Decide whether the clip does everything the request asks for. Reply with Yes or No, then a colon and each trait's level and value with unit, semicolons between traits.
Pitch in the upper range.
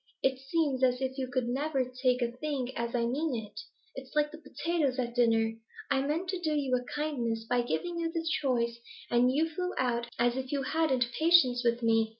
Yes: very high, 260 Hz